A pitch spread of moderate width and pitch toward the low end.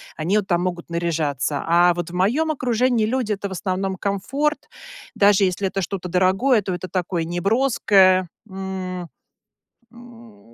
No: average, 3.5 semitones; high, 190 Hz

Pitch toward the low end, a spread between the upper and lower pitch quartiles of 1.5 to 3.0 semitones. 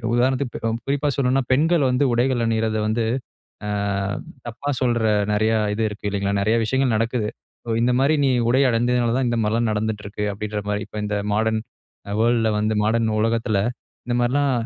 Yes: low, 115 Hz; average, 2.7 semitones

